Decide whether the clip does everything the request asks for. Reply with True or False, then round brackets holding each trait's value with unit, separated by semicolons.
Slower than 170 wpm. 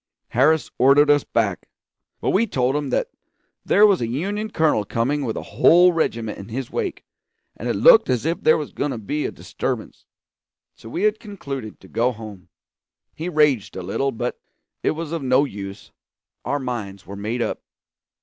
False (180 wpm)